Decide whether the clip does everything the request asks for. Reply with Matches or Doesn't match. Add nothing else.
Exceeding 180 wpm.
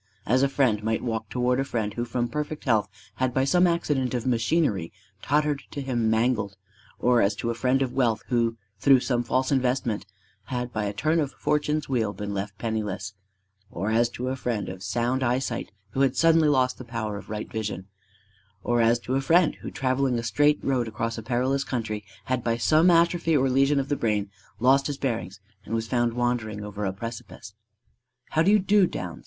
Matches